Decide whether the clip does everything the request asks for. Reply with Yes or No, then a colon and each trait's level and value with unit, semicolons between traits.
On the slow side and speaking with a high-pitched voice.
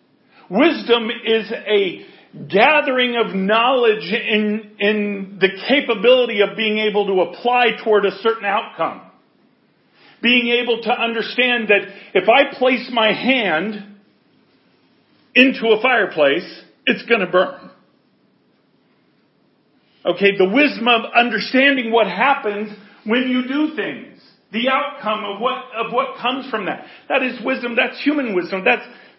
Yes: slow, 130 wpm; high, 235 Hz